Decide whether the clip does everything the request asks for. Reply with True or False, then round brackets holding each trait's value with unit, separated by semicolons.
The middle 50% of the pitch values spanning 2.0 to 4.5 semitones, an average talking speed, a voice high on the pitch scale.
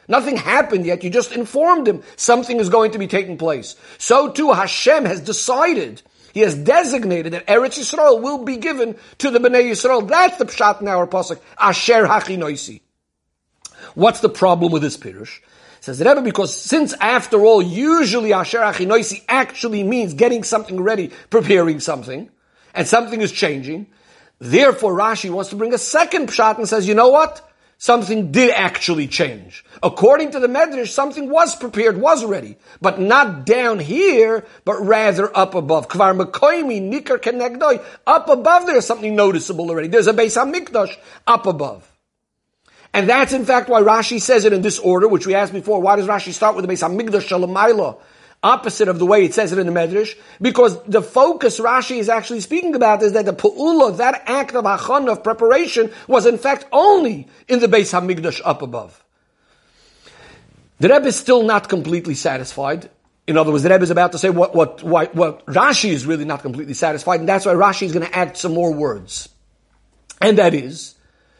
False (5.2 semitones; 180 wpm; 220 Hz)